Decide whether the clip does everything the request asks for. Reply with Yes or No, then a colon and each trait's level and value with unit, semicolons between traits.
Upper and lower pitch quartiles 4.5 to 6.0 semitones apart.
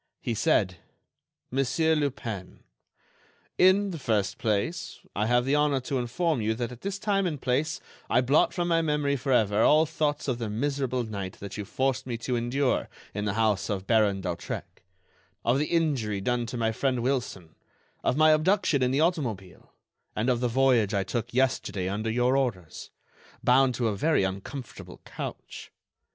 Yes: average, 5.0 semitones